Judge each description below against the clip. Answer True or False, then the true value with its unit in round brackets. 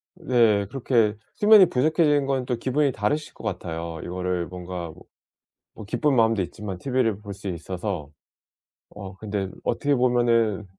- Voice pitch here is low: True (110 Hz)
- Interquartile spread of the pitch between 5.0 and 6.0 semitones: True (5.6 semitones)